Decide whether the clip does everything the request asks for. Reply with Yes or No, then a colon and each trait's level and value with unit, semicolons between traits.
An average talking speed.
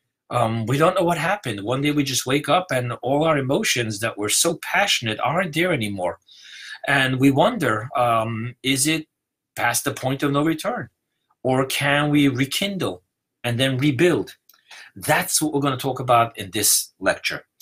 Yes: average, 175 wpm